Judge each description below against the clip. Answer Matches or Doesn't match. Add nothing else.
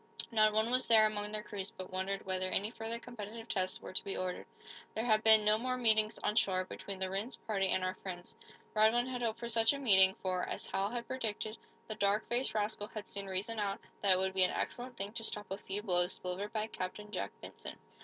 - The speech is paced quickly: Matches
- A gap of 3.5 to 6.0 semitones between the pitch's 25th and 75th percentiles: Doesn't match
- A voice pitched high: Matches